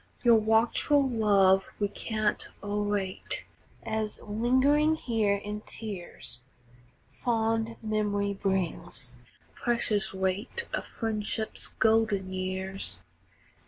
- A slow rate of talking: Yes, slow, 90 wpm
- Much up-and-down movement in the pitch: No, narrow, 2.5 semitones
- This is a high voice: Yes, high, 210 Hz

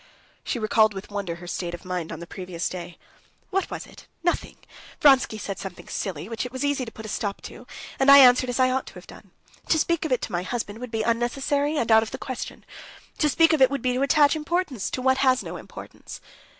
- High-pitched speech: Yes, high, 245 Hz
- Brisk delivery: Yes, fast, 240 wpm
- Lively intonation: Yes, wide, 5.7 semitones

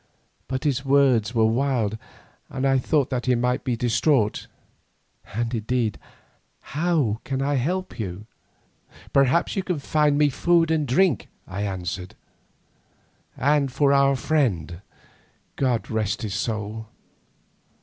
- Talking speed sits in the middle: No, slow, 130 wpm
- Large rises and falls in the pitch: No, average, 4.4 semitones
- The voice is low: Yes, low, 130 Hz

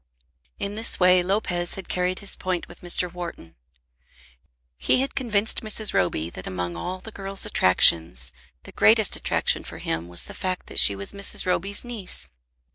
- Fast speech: No, average, 170 wpm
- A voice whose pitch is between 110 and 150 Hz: No, medium, 180 Hz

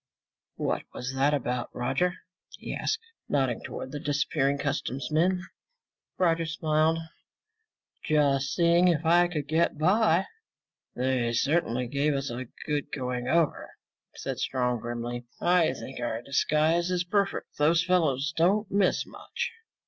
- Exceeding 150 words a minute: No, slow, 135 wpm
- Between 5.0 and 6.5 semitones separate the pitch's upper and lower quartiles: No, average, 4.5 semitones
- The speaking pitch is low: No, medium, 150 Hz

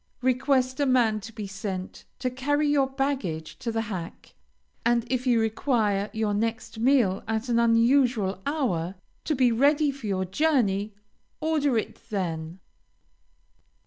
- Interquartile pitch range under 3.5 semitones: No, average, 4.7 semitones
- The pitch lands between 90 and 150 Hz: No, high, 230 Hz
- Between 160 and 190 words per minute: No, average, 145 wpm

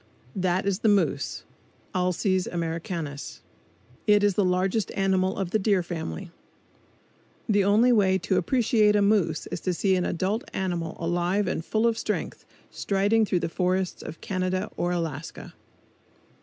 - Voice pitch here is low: No, medium, 185 Hz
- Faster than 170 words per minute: No, average, 150 wpm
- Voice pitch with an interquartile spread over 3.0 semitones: No, average, 2.7 semitones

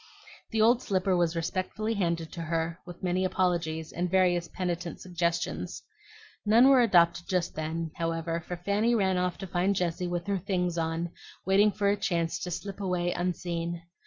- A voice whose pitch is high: No, medium, 175 Hz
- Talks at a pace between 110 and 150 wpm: No, average, 170 wpm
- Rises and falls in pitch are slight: Yes, narrow, 2.1 semitones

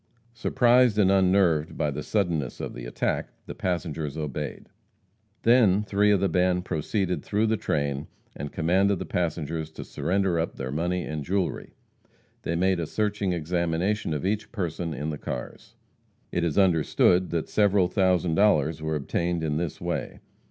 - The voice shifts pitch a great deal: No, average, 3.9 semitones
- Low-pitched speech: Yes, very low, 90 Hz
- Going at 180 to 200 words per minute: No, average, 165 wpm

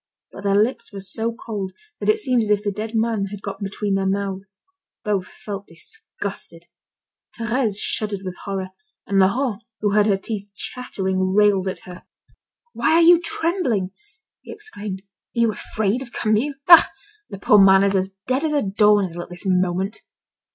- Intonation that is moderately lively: Yes, average, 3.1 semitones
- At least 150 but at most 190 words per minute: Yes, average, 175 wpm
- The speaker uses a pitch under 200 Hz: No, high, 205 Hz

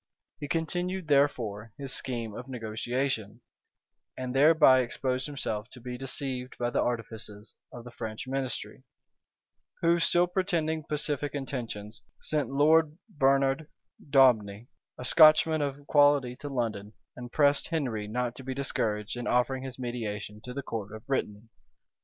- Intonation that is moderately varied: Yes, average, 3.8 semitones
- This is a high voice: No, low, 130 Hz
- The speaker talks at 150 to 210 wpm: No, average, 140 wpm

